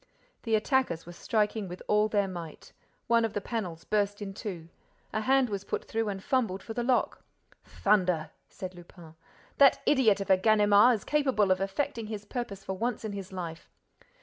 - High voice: Yes, high, 205 Hz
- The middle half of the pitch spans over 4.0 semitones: No, average, 3.3 semitones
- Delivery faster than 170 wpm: Yes, average, 185 wpm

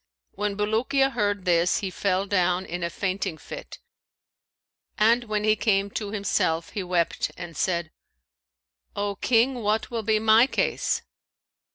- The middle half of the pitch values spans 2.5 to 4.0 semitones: Yes, average, 3.1 semitones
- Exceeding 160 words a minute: No, average, 145 wpm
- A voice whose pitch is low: No, high, 205 Hz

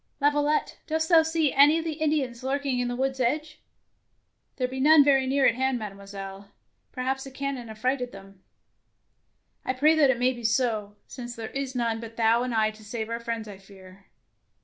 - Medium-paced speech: No, fast, 210 wpm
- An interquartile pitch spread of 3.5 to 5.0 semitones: Yes, average, 3.9 semitones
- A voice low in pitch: No, very high, 250 Hz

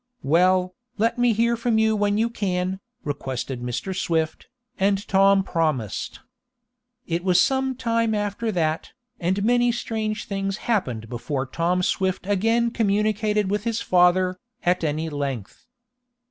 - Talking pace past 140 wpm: No, slow, 135 wpm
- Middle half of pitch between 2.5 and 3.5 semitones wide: No, average, 4.6 semitones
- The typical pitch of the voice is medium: No, high, 195 Hz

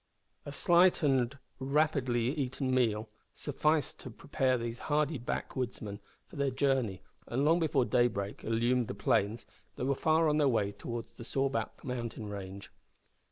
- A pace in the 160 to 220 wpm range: No, average, 150 wpm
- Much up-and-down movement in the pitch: No, average, 3.7 semitones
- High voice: No, low, 130 Hz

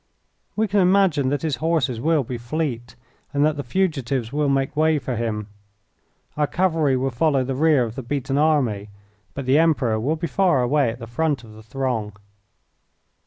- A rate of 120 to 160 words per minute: No, average, 185 wpm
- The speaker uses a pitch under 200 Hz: Yes, low, 135 Hz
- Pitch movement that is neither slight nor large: Yes, average, 4.5 semitones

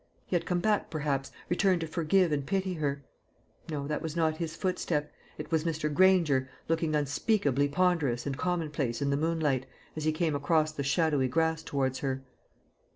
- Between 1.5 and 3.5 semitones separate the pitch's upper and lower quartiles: Yes, average, 3.1 semitones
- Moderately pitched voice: Yes, medium, 155 Hz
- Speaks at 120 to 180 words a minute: Yes, average, 175 wpm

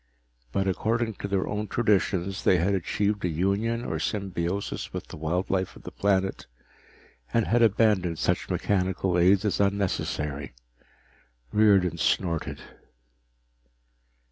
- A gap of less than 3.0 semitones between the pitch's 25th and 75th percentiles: Yes, narrow, 2.6 semitones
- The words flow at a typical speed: No, slow, 125 wpm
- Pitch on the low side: Yes, very low, 95 Hz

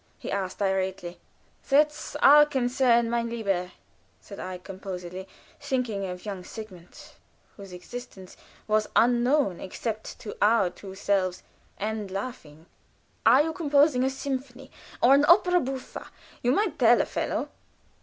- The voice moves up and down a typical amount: No, wide, 5.7 semitones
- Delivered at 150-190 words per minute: No, slow, 135 wpm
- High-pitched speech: Yes, high, 225 Hz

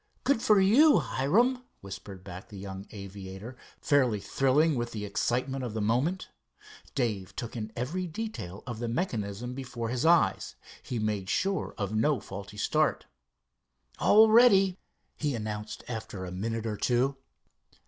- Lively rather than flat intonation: Yes, wide, 6.8 semitones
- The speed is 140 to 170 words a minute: Yes, average, 150 wpm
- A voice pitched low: Yes, low, 120 Hz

